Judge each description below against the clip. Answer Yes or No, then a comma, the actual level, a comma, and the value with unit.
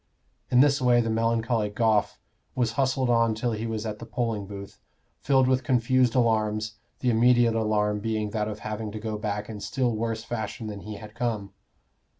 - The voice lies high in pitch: No, low, 115 Hz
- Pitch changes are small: Yes, narrow, 2.2 semitones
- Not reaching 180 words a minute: No, average, 185 wpm